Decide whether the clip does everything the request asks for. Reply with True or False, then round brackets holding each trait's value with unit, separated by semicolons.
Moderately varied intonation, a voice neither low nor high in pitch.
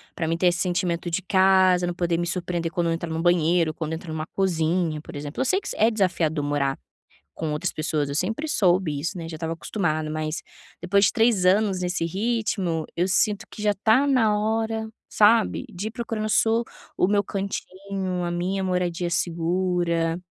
True (3.3 semitones; 180 Hz)